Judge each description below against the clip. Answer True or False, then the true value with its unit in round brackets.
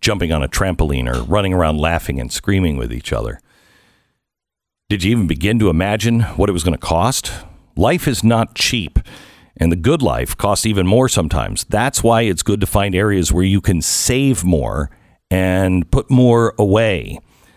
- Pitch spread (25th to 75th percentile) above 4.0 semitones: True (4.8 semitones)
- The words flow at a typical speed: True (180 wpm)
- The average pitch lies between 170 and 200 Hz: False (95 Hz)